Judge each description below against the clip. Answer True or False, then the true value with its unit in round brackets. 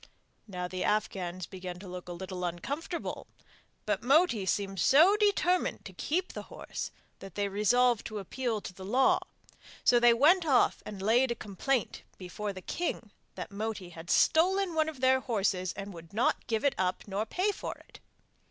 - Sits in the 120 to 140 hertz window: False (215 Hz)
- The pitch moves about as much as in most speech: False (6.3 semitones)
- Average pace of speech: True (180 wpm)